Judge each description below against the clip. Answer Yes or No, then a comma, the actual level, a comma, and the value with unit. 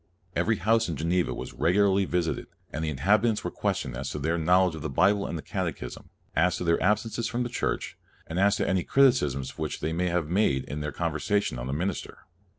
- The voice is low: Yes, very low, 90 Hz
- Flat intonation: No, average, 4.7 semitones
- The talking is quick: Yes, fast, 215 wpm